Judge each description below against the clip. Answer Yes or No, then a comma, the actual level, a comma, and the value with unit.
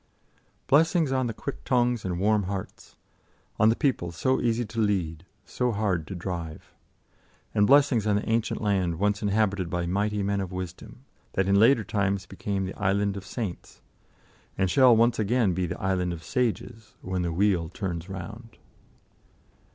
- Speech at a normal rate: Yes, average, 165 wpm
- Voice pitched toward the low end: Yes, low, 100 Hz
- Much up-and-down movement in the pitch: No, average, 3.6 semitones